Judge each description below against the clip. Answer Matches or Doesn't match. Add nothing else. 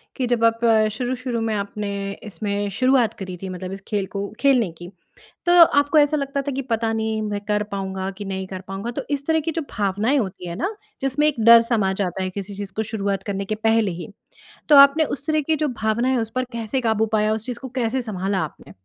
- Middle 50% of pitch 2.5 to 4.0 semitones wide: Doesn't match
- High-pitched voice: Matches